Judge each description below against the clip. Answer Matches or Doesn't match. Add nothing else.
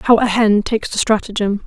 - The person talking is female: Matches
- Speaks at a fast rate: Matches